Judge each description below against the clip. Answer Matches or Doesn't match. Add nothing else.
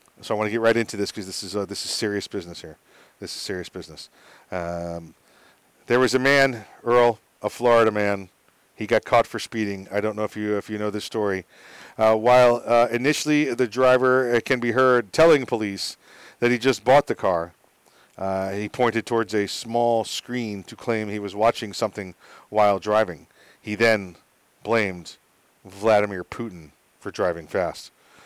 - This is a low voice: Matches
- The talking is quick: Doesn't match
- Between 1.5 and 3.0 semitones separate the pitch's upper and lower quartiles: Doesn't match